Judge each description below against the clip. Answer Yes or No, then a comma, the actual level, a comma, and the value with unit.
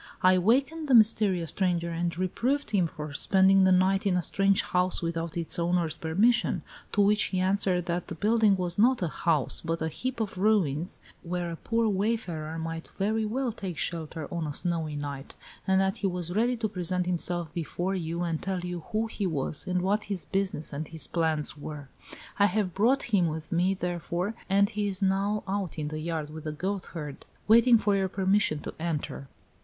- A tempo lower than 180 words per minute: No, average, 195 wpm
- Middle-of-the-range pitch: Yes, medium, 180 Hz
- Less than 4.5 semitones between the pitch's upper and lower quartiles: Yes, average, 3.6 semitones